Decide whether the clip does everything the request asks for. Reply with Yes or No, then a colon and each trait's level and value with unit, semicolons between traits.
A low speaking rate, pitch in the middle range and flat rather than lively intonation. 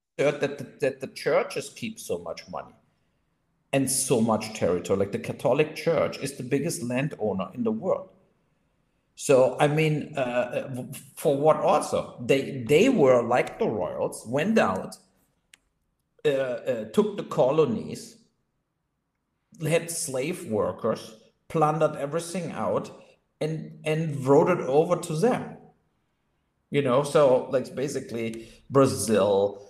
No: slow, 125 wpm; medium, 155 Hz; average, 4.4 semitones